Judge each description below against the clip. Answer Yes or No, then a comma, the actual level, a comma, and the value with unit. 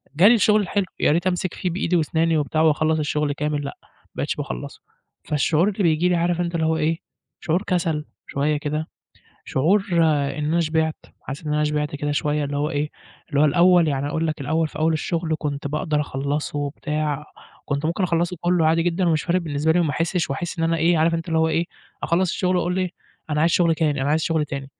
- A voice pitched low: No, medium, 160 Hz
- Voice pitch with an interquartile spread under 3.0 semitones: Yes, narrow, 2.4 semitones